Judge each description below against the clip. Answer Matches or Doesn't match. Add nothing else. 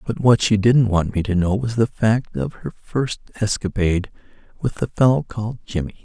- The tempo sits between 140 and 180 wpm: Doesn't match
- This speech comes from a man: Matches